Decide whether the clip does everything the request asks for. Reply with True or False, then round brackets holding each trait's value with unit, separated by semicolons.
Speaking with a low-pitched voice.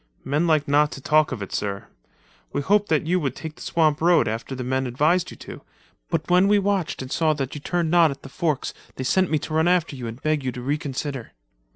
False (150 Hz)